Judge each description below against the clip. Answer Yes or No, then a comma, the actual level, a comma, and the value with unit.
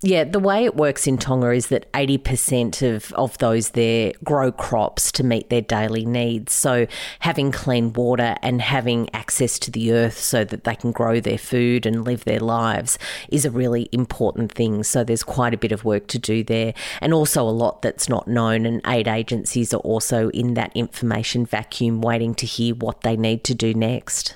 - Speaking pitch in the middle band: No, low, 120 Hz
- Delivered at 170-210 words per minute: Yes, average, 200 wpm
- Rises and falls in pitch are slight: Yes, narrow, 1.8 semitones